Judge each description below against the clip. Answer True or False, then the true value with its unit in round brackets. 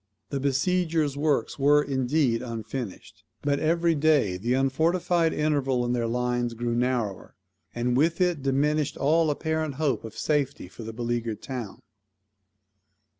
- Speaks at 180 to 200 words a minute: False (135 wpm)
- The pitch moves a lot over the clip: False (4.3 semitones)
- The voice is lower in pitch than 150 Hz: True (135 Hz)